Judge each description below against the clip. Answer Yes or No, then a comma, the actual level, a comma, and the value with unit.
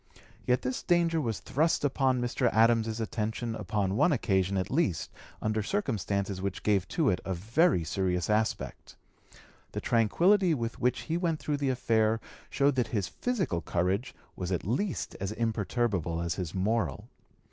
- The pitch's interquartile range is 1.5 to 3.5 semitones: No, wide, 5.4 semitones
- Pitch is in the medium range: No, low, 115 Hz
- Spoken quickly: No, average, 150 wpm